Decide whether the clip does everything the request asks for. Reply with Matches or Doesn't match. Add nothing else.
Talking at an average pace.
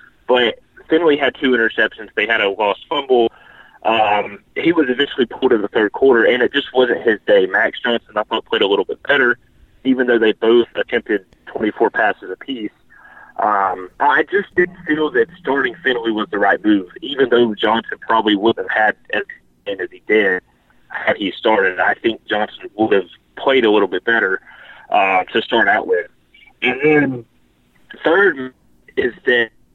Matches